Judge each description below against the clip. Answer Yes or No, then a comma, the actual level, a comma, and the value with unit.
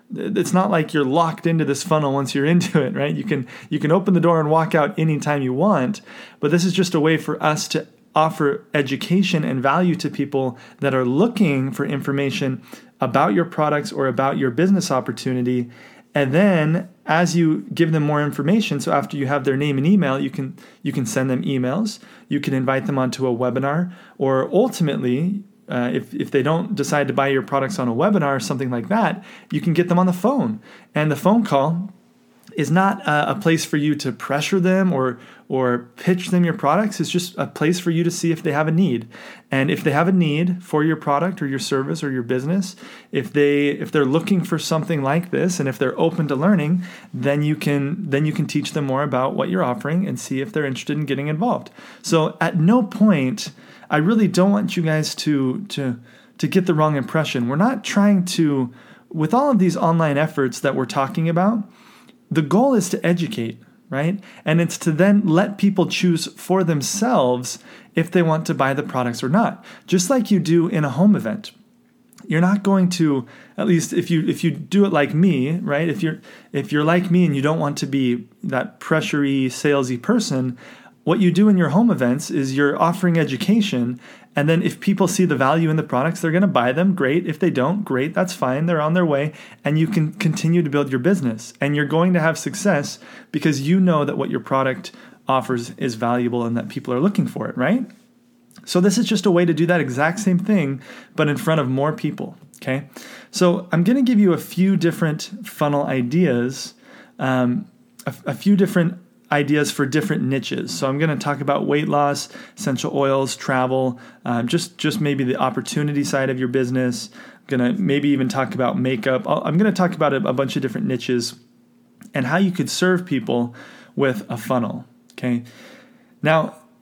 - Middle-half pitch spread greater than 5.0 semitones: Yes, wide, 5.5 semitones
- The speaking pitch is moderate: Yes, medium, 160 Hz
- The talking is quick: Yes, fast, 210 wpm